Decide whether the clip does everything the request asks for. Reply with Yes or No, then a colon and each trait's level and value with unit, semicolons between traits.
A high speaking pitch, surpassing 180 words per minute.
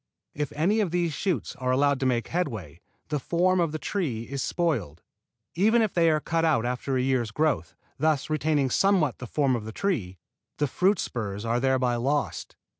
No: medium, 145 Hz; average, 190 wpm